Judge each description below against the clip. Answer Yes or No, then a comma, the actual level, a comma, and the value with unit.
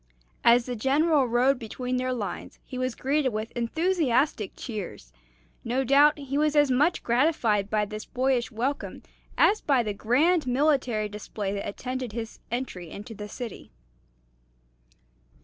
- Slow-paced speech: No, average, 145 wpm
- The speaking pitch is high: Yes, very high, 250 Hz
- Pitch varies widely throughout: No, average, 4.2 semitones